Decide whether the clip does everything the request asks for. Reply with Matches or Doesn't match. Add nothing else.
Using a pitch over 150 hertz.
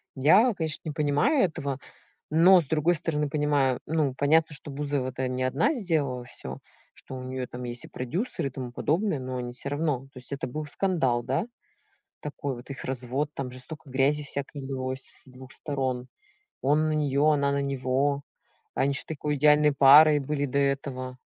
Doesn't match